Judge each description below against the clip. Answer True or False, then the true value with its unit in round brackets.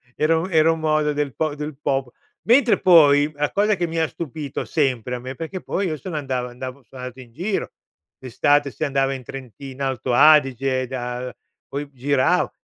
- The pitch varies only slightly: False (3.4 semitones)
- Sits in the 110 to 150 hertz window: True (140 Hz)